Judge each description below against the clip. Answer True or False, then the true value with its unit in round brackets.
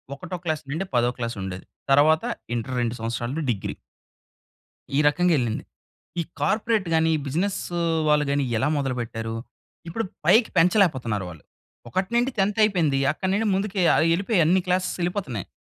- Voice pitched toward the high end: False (155 Hz)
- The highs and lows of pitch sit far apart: True (7.5 semitones)